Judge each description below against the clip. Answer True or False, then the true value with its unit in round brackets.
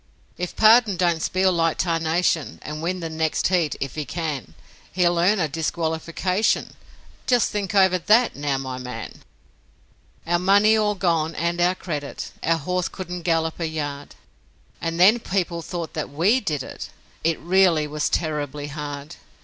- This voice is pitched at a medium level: True (170 Hz)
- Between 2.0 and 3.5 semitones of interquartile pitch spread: True (3.2 semitones)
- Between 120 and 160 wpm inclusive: True (155 wpm)